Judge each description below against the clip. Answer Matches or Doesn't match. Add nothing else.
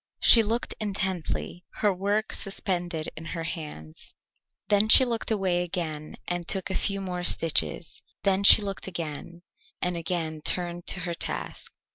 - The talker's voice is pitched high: Doesn't match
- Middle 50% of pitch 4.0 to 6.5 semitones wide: Doesn't match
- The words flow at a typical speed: Matches